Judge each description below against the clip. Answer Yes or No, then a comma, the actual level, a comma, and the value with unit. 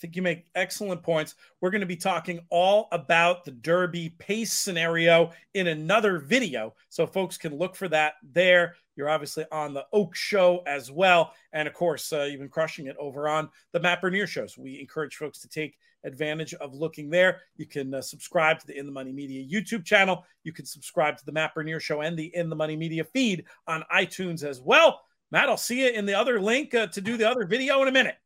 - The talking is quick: Yes, fast, 225 wpm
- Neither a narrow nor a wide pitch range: Yes, average, 3.8 semitones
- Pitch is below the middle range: No, medium, 170 Hz